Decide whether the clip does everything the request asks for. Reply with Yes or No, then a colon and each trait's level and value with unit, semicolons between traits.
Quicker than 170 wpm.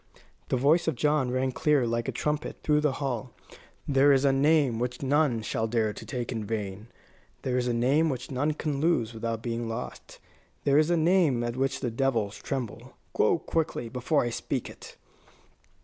Yes: average, 190 wpm